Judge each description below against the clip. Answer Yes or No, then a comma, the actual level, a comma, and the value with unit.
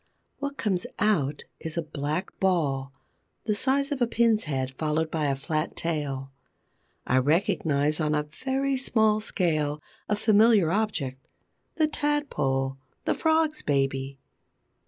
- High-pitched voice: No, medium, 160 Hz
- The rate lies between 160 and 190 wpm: No, slow, 135 wpm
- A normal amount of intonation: No, wide, 7.6 semitones